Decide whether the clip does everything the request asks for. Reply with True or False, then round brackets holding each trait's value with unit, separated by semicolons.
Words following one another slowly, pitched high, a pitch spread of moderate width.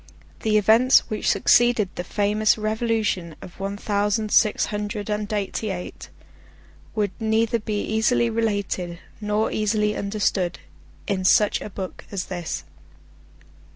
False (125 wpm; 210 Hz; 1.7 semitones)